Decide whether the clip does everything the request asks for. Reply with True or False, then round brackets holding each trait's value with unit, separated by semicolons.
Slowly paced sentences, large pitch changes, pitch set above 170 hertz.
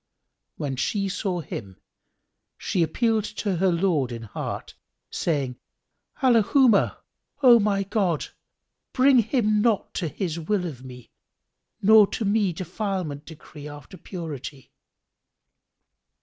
True (115 wpm; 6.0 semitones; 185 Hz)